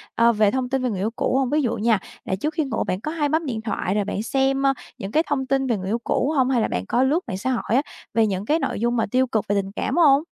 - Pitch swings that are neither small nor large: Yes, average, 4.3 semitones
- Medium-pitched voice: No, very high, 250 Hz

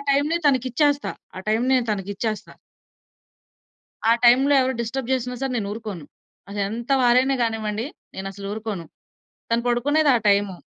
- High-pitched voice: Yes, high, 235 Hz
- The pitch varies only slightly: No, average, 3.9 semitones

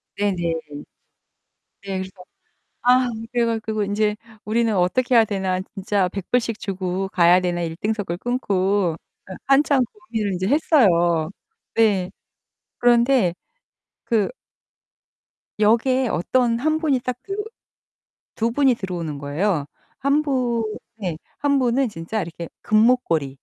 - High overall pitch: Yes, high, 210 Hz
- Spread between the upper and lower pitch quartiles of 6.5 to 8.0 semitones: No, average, 5.1 semitones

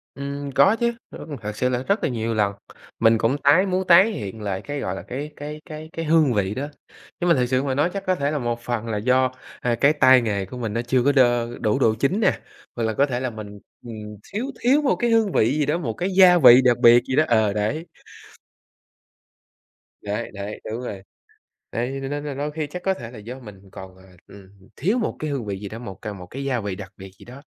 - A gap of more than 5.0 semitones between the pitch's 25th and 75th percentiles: Yes, wide, 5.4 semitones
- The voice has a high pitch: No, low, 125 Hz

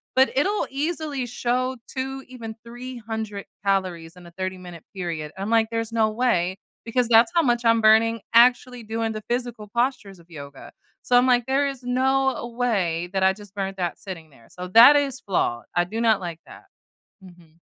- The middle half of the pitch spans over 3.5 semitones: Yes, average, 5.0 semitones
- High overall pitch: Yes, high, 225 Hz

